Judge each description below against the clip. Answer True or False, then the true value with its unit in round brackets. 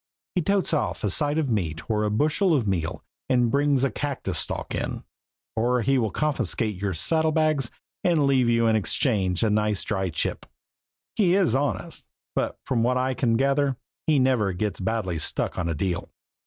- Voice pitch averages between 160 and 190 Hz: False (120 Hz)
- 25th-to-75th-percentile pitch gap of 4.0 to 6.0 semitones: True (5.5 semitones)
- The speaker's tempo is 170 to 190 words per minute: True (180 wpm)